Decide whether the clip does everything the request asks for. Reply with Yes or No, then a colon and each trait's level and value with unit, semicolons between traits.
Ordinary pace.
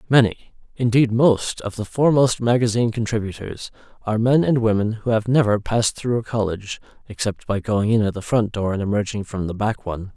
Yes: average, 195 wpm